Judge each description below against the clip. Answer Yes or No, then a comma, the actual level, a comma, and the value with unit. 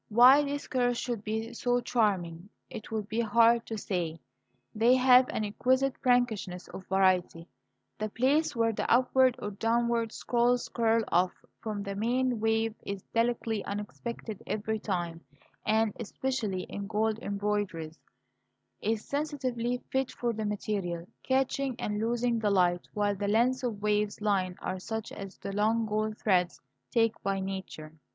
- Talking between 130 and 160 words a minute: Yes, average, 150 wpm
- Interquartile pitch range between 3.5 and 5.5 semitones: No, average, 3.1 semitones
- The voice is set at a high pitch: Yes, high, 220 Hz